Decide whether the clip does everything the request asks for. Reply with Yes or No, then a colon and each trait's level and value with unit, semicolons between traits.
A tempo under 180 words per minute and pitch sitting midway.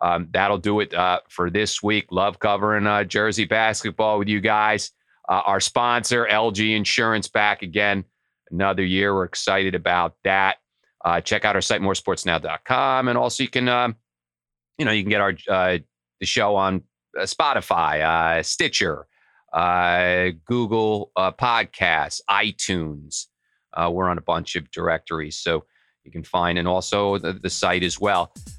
No: average, 160 wpm; very low, 95 Hz